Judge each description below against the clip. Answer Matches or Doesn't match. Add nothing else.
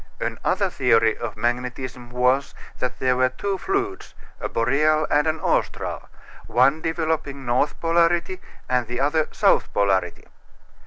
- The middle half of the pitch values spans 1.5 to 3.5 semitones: Doesn't match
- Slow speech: Matches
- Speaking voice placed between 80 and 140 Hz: Matches